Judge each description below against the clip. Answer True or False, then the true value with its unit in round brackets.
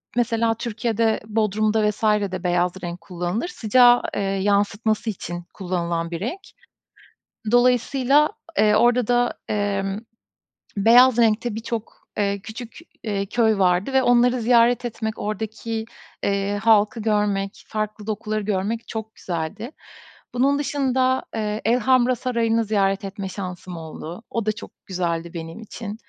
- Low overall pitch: False (215 Hz)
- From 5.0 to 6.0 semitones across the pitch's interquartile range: False (3.1 semitones)